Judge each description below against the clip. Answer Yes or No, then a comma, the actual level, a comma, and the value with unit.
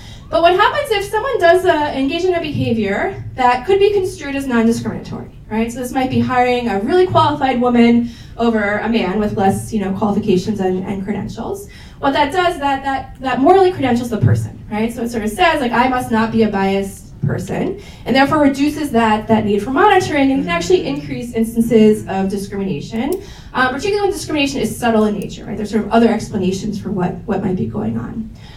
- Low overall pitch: No, high, 235 Hz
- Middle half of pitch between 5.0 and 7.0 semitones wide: Yes, wide, 5.6 semitones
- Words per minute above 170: Yes, fast, 205 wpm